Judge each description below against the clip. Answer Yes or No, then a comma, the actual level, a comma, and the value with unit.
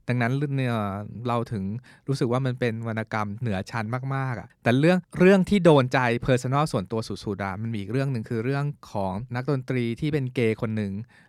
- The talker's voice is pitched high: No, low, 120 Hz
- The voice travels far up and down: No, average, 3.7 semitones